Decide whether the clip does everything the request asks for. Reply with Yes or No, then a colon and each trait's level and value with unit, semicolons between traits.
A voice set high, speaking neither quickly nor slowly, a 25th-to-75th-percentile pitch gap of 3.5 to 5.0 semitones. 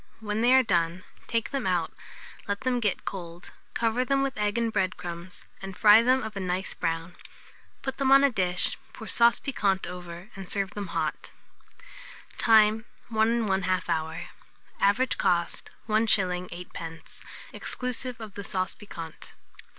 Yes: high, 200 Hz; average, 155 wpm; average, 4.3 semitones